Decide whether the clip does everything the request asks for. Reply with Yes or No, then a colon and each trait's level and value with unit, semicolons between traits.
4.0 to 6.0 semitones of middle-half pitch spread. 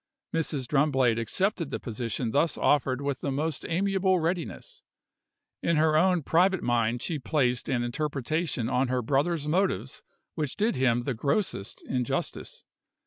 Yes: average, 5.1 semitones